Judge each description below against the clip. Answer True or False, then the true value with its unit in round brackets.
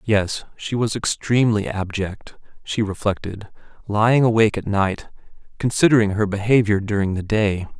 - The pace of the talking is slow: True (130 wpm)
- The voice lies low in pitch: True (105 Hz)